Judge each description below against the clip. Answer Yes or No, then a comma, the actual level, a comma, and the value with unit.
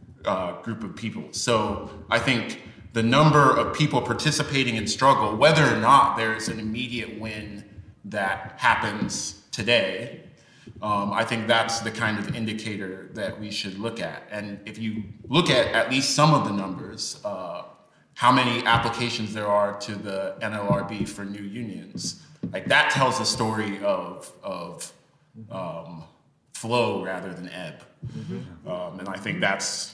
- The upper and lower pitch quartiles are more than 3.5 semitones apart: No, average, 2.7 semitones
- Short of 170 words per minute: Yes, average, 155 wpm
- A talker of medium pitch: No, low, 110 Hz